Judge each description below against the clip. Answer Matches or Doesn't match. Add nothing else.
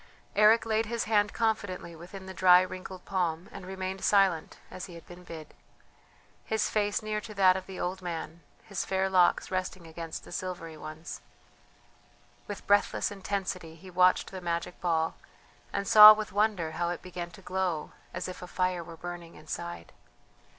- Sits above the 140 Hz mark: Matches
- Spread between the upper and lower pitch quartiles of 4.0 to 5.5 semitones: Doesn't match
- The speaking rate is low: Doesn't match